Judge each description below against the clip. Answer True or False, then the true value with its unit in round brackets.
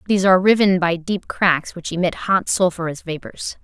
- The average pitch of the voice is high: False (180 Hz)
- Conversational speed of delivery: True (180 wpm)